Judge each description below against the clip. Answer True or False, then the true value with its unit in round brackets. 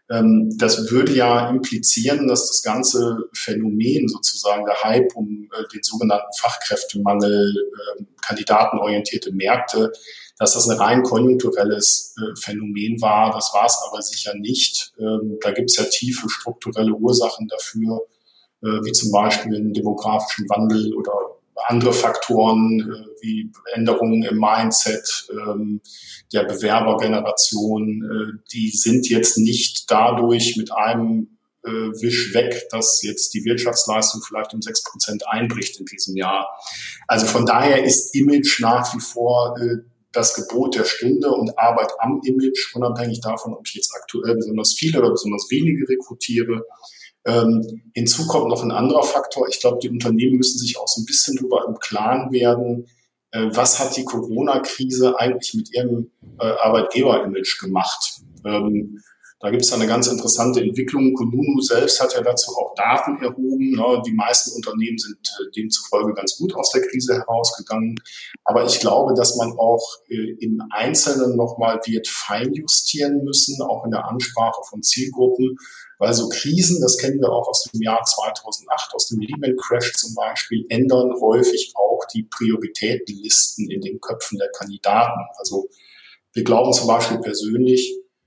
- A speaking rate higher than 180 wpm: False (145 wpm)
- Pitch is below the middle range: True (120 Hz)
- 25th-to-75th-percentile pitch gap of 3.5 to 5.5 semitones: False (2.7 semitones)